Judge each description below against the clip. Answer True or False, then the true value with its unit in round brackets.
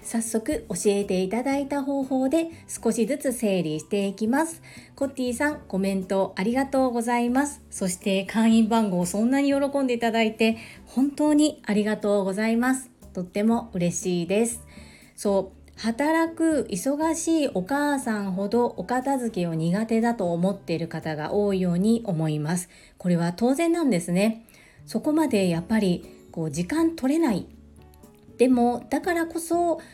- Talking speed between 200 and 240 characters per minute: False (315 characters per minute)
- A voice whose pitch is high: True (225 Hz)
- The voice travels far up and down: True (6.2 semitones)